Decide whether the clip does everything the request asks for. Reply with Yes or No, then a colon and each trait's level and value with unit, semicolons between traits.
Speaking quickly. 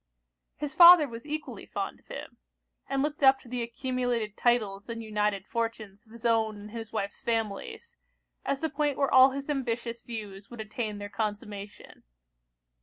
No: average, 170 wpm